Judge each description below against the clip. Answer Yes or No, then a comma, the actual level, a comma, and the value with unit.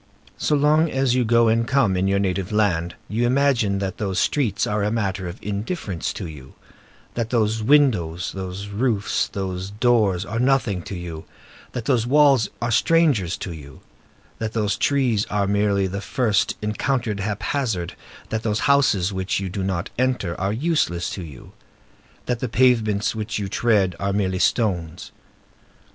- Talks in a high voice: No, low, 105 Hz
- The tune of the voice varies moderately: Yes, average, 4.2 semitones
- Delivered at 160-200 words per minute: Yes, average, 165 wpm